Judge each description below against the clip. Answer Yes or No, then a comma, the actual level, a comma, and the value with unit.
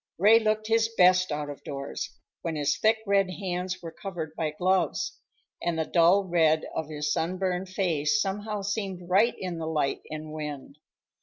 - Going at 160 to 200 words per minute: Yes, average, 170 wpm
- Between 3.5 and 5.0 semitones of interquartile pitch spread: Yes, average, 3.9 semitones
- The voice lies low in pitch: No, medium, 180 Hz